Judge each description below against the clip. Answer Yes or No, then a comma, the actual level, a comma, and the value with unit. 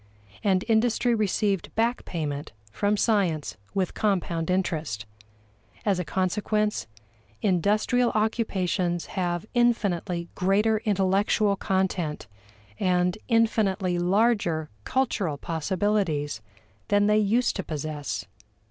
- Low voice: No, high, 195 Hz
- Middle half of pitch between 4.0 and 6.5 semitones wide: No, average, 3.5 semitones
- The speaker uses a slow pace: Yes, slow, 95 wpm